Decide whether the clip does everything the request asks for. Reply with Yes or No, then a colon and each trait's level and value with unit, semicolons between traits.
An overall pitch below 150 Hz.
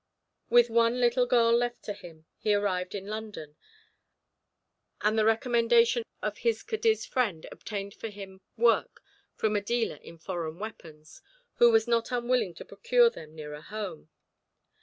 No: high, 220 Hz